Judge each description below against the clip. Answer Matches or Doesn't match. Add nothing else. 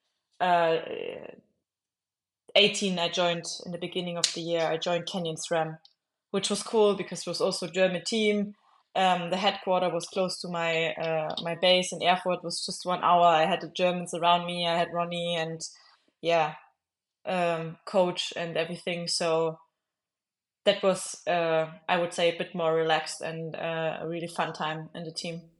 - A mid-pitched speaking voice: Matches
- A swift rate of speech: Doesn't match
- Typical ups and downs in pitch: Doesn't match